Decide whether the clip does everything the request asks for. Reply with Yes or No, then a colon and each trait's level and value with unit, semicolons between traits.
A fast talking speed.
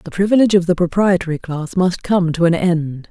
Yes: fast, 215 wpm